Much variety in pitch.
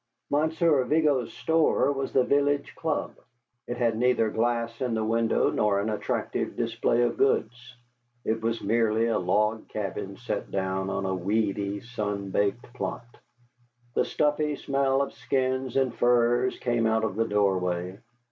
No: average, 3.7 semitones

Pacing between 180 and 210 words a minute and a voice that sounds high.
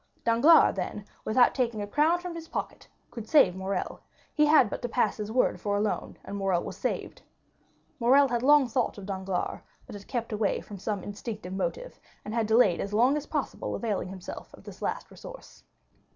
Yes: average, 195 wpm; high, 225 Hz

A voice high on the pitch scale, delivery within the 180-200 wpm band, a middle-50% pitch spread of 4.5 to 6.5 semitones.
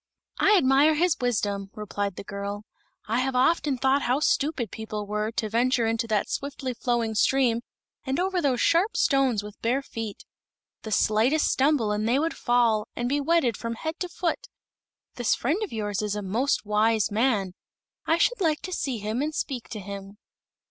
Yes: high, 240 Hz; average, 185 wpm; average, 4.9 semitones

